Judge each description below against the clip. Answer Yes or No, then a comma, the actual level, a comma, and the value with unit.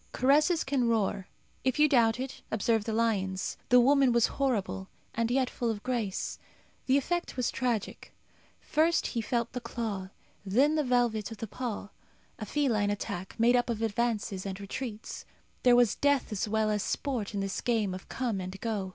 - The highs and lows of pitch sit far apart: No, average, 3.7 semitones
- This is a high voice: Yes, high, 230 Hz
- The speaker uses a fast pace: No, average, 180 wpm